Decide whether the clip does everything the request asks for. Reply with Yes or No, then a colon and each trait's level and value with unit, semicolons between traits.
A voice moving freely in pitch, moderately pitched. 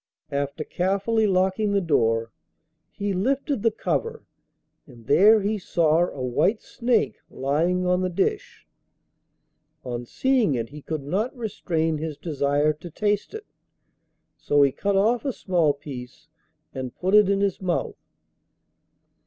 Yes: wide, 6.4 semitones; medium, 180 Hz